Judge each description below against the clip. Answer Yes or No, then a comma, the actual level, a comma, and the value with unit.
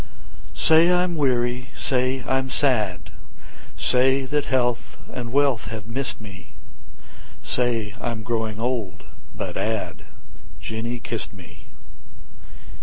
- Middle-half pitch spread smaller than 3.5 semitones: Yes, average, 3.0 semitones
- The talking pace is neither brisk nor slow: No, slow, 110 wpm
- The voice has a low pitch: Yes, low, 120 Hz